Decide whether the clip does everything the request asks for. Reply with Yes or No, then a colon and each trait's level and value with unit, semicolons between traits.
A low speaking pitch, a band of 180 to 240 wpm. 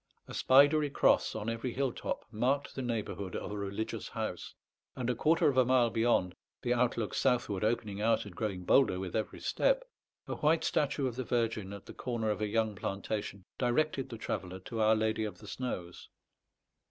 Yes: low, 115 Hz; average, 190 wpm